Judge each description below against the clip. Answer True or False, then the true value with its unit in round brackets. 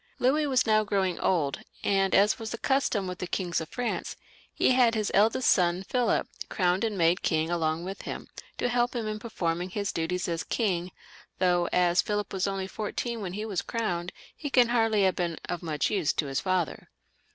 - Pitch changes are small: False (4.1 semitones)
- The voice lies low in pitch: False (195 Hz)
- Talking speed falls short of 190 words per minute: False (200 wpm)